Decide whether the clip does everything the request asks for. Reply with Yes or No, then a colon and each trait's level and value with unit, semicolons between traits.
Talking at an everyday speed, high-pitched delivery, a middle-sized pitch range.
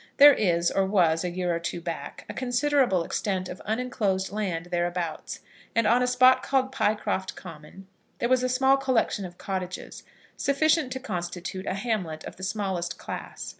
No: average, 170 wpm; high, 195 Hz; wide, 6.1 semitones